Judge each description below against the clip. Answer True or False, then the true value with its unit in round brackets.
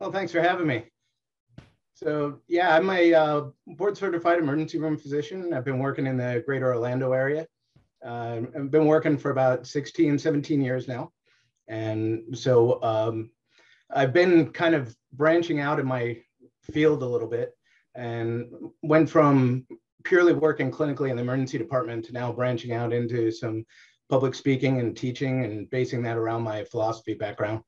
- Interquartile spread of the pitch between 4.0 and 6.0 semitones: True (4.7 semitones)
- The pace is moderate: True (165 wpm)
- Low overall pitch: True (130 Hz)